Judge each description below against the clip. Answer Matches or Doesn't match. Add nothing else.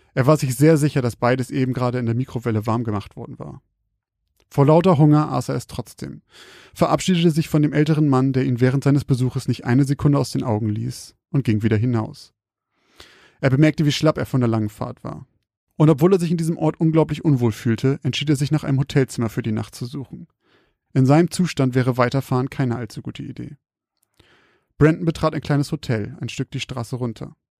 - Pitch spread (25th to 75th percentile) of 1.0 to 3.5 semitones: Doesn't match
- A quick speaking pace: Matches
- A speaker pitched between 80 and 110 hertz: Doesn't match